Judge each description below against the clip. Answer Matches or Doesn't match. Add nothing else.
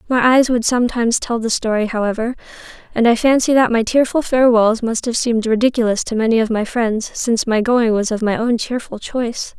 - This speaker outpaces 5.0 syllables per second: Matches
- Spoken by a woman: Matches